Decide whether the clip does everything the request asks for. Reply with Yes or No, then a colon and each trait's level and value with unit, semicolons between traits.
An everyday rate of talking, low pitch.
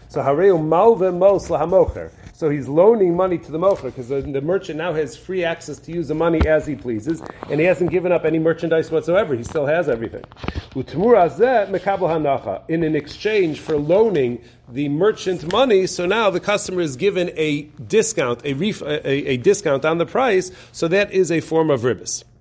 No: average, 175 wpm; medium, 165 Hz